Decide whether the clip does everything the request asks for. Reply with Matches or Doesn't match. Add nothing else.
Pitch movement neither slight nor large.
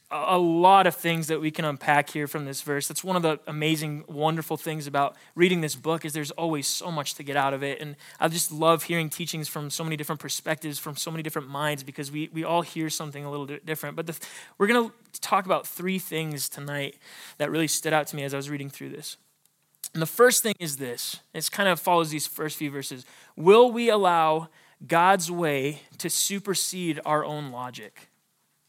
Doesn't match